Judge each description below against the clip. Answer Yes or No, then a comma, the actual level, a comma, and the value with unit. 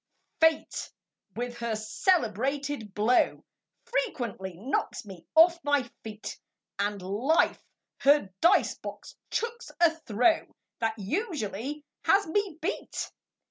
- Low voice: No, very high, 275 Hz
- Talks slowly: Yes, slow, 105 wpm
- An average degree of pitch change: No, wide, 7.5 semitones